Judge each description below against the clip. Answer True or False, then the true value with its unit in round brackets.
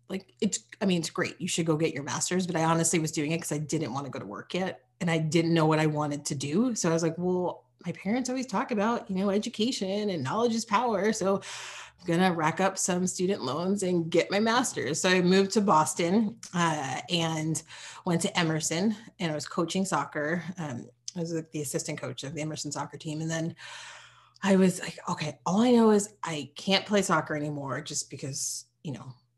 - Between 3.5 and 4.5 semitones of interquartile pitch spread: True (4.0 semitones)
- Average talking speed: False (230 wpm)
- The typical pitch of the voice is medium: True (170 Hz)